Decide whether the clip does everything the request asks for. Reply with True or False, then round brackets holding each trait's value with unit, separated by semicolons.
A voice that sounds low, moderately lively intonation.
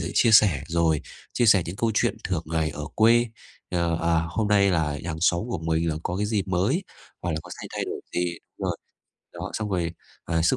True (85 Hz; 4.1 semitones)